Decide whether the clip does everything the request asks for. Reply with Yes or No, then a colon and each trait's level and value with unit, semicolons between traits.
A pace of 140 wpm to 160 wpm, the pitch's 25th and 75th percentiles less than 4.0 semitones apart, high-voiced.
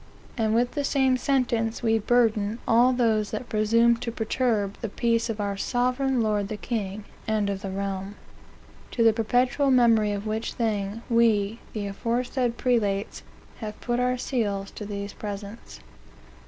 Yes: average, 155 wpm; average, 2.9 semitones; high, 225 Hz